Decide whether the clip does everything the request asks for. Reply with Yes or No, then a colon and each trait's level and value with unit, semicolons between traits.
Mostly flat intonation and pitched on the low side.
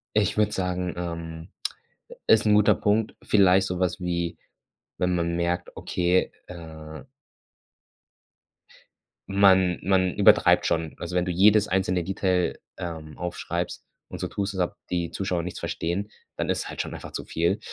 Yes: narrow, 2.2 semitones; very low, 90 Hz